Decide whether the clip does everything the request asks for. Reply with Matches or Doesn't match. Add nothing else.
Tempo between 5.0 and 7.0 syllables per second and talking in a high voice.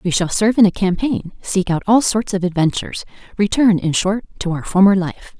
Matches